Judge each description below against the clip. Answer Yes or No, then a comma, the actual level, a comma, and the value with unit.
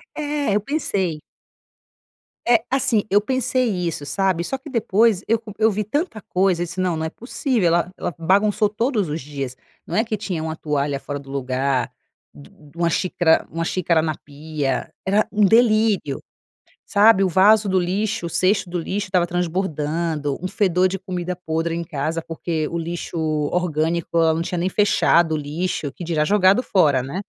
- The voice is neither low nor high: Yes, medium, 180 Hz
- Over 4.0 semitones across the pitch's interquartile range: Yes, average, 4.6 semitones